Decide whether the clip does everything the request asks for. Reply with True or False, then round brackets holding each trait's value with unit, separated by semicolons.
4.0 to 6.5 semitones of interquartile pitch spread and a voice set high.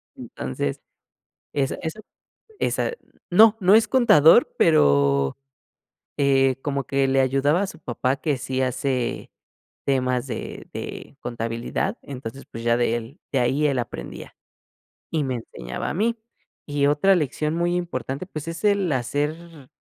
False (4.7 semitones; 140 Hz)